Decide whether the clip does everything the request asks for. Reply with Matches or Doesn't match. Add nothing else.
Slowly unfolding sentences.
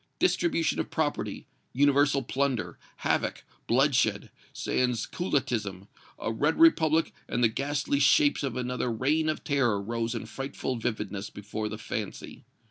Matches